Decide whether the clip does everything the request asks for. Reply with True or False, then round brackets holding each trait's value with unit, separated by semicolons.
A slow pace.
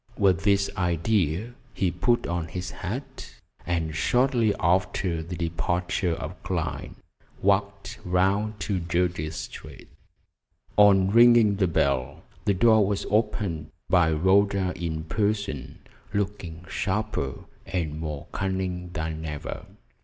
True (115 wpm)